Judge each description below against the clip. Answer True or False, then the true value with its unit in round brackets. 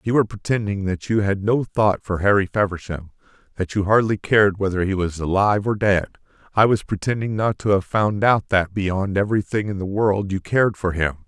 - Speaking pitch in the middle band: False (100 Hz)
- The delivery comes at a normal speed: False (210 wpm)